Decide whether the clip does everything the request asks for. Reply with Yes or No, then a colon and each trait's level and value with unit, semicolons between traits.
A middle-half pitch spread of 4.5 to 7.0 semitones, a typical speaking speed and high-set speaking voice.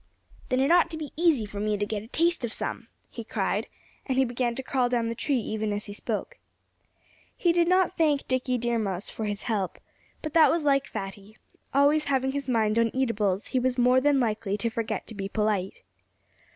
No: average, 4.8 semitones; fast, 215 wpm; high, 245 Hz